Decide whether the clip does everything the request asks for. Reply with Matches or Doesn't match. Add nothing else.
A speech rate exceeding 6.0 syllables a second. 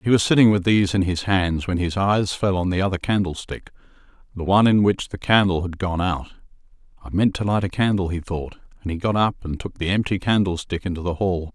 Doesn't match